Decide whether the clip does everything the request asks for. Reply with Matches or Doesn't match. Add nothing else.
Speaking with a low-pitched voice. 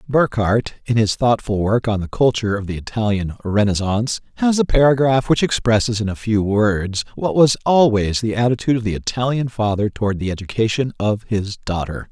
Matches